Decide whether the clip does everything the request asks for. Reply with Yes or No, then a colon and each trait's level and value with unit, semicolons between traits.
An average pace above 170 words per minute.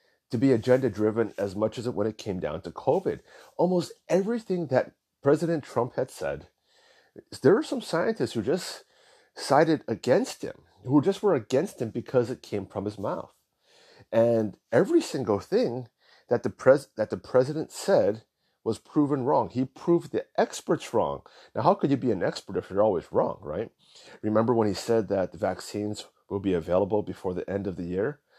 Yes: average, 185 wpm